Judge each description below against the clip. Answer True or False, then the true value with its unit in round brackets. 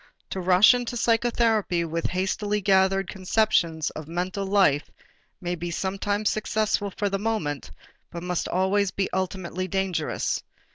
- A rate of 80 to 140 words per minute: True (135 wpm)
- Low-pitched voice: False (190 Hz)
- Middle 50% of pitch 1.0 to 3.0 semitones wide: True (2.7 semitones)